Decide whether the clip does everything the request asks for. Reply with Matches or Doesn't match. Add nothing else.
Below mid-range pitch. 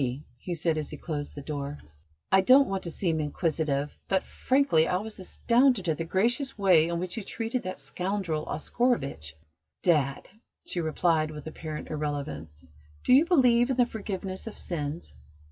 Doesn't match